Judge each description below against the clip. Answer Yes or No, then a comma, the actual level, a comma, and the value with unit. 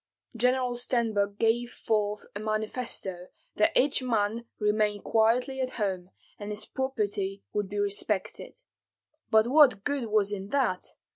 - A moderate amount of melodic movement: Yes, average, 3.2 semitones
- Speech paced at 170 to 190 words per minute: No, slow, 135 wpm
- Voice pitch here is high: Yes, high, 215 Hz